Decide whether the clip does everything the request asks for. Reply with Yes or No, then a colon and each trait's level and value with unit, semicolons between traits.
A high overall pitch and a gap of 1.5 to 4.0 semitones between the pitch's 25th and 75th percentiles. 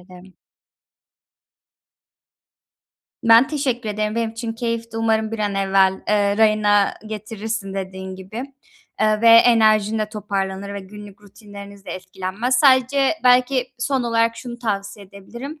Yes: high, 215 Hz; narrow, 2.6 semitones